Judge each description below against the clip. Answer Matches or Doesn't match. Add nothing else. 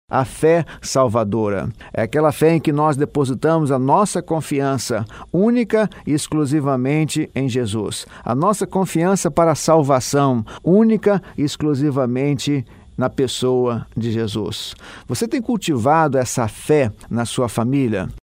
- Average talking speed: Matches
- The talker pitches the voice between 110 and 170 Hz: Matches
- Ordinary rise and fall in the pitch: Matches